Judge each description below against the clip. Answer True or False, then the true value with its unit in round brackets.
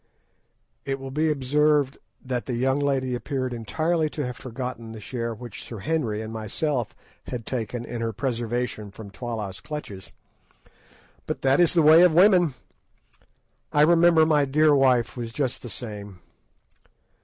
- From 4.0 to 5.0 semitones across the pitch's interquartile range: True (4.5 semitones)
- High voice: False (130 Hz)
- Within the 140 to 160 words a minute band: True (155 wpm)